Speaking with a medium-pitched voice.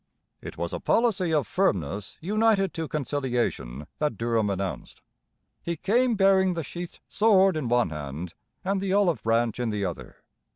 Yes: medium, 150 Hz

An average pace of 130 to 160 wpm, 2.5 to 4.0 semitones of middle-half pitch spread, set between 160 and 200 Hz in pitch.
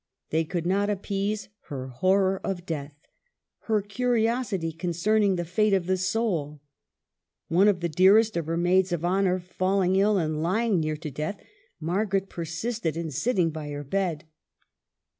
Yes: average, 155 wpm; average, 3.6 semitones; medium, 185 Hz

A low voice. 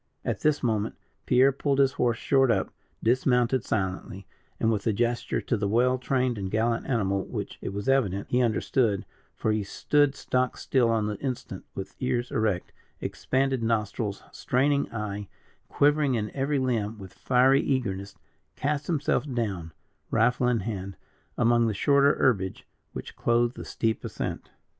Yes: low, 120 Hz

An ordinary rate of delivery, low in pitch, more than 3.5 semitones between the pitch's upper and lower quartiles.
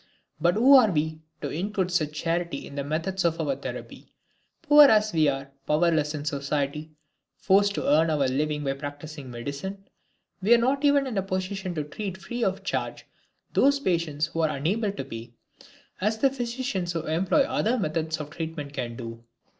No: average, 180 wpm; medium, 165 Hz; wide, 5.4 semitones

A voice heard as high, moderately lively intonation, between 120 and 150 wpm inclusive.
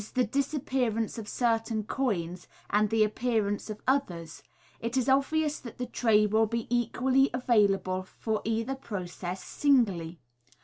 Yes: high, 225 Hz; average, 3.7 semitones; average, 140 wpm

